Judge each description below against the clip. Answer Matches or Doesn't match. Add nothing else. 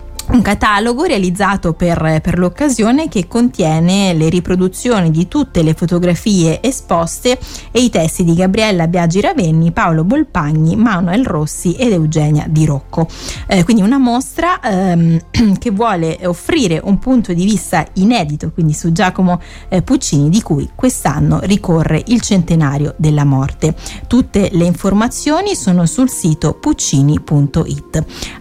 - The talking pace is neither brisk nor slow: Matches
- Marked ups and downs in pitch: Matches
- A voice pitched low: Doesn't match